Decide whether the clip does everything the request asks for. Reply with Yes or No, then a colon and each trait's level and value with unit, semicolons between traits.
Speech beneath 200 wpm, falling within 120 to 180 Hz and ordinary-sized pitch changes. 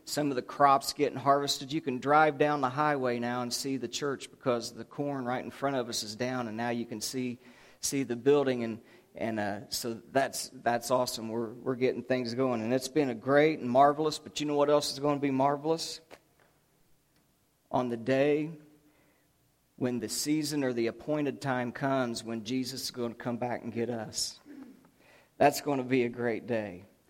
No: fast, 205 wpm; low, 130 Hz; average, 3.2 semitones